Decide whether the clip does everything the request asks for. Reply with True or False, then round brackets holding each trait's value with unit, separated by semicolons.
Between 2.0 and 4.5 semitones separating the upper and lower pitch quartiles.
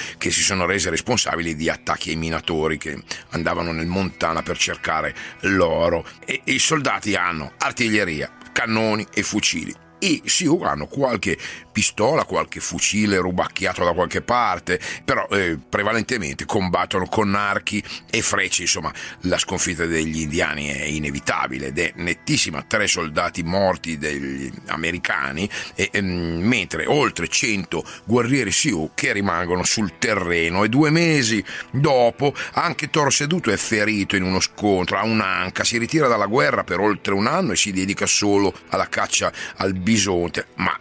True (4.2 semitones)